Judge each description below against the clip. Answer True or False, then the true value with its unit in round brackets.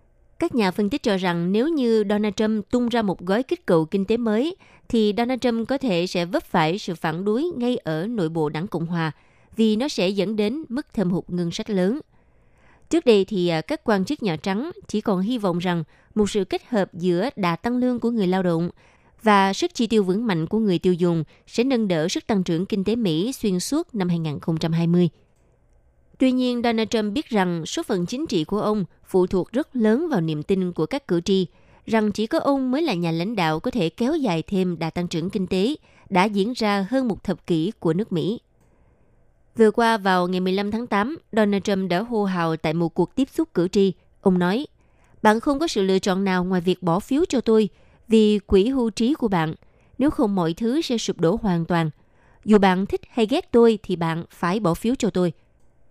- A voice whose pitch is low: False (200 Hz)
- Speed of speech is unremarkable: True (225 wpm)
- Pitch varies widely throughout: False (4.8 semitones)